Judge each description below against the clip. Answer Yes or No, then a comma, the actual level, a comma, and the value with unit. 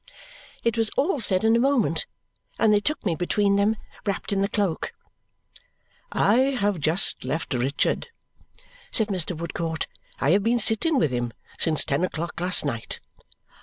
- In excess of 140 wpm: Yes, average, 160 wpm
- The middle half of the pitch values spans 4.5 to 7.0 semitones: Yes, wide, 5.5 semitones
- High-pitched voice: Yes, high, 195 Hz